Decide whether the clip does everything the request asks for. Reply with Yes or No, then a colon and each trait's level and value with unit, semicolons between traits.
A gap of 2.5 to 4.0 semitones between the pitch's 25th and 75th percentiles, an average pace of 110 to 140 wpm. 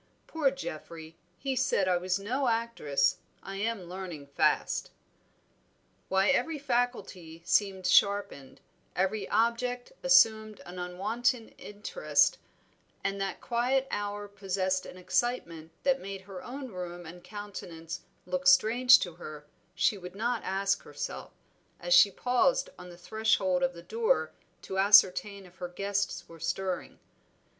No: average, 4.8 semitones; slow, 135 wpm